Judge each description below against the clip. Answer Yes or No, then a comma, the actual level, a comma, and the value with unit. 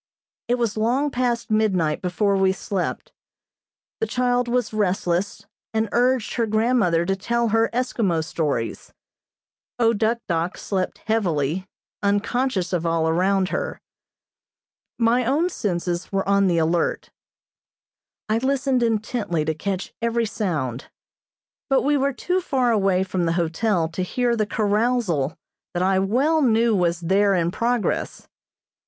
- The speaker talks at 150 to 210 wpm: No, slow, 135 wpm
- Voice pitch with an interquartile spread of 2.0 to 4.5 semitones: No, average, 5.0 semitones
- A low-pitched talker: No, high, 205 Hz